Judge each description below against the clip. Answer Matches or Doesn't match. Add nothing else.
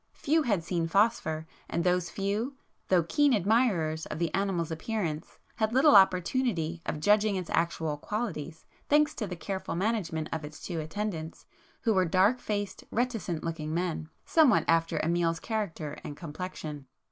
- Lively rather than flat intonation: Doesn't match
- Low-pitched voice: Doesn't match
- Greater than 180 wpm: Doesn't match